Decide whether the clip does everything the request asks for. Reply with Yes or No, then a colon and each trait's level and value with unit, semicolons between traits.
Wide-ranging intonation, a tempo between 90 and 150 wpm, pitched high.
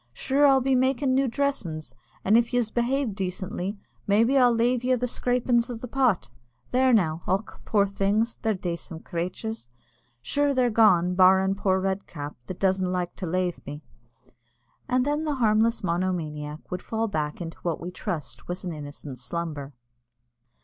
No: wide, 6.0 semitones; average, 170 wpm; high, 195 Hz